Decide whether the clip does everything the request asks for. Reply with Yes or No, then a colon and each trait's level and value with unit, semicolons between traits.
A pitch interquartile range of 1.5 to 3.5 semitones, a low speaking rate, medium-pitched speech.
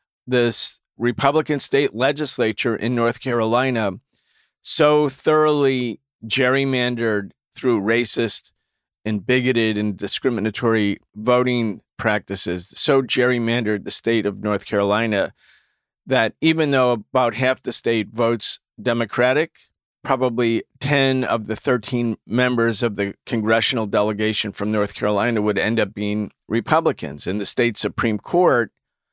No: average, 3.1 semitones; slow, 115 wpm; low, 115 Hz